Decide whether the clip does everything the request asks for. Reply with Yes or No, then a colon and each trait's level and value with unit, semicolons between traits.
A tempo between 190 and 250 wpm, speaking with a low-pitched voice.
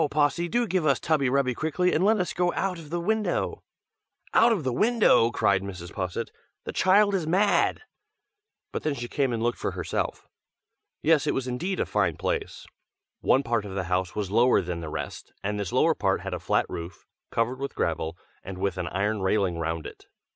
Yes: fast, 205 wpm; low, 125 Hz